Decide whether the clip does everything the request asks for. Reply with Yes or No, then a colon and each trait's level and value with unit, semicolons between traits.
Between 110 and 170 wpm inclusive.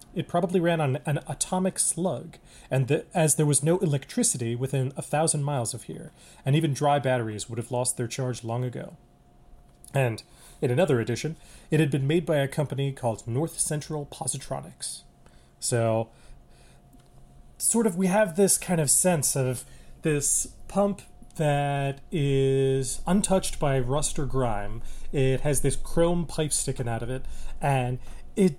Yes: average, 160 wpm